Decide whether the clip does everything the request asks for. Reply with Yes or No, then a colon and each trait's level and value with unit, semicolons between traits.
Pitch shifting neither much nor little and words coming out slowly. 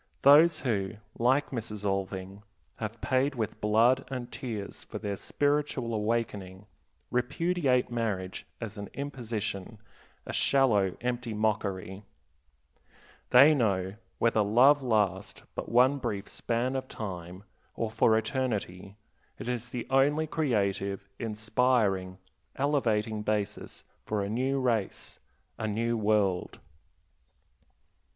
Yes: average, 4.0 semitones; slow, 115 wpm